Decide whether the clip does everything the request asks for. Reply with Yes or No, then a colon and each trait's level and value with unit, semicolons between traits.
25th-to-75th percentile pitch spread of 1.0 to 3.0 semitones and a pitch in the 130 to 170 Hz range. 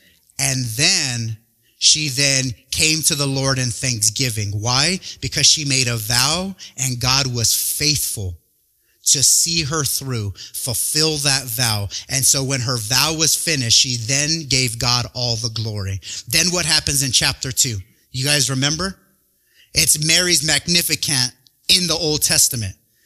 No: average, 4.3 semitones; low, 135 Hz